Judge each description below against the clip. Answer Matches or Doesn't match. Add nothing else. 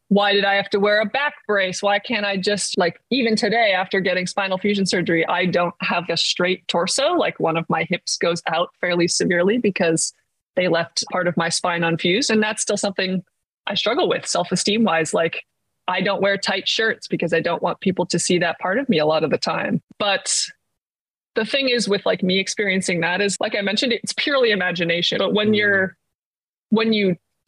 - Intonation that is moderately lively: Matches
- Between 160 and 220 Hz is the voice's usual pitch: Matches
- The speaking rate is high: Matches